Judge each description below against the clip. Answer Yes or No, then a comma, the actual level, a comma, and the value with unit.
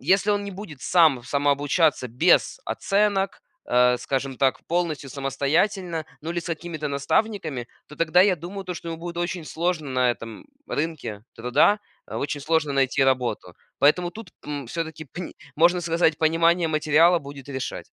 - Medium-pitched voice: Yes, medium, 160 Hz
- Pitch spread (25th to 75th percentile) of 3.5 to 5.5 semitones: Yes, average, 4.0 semitones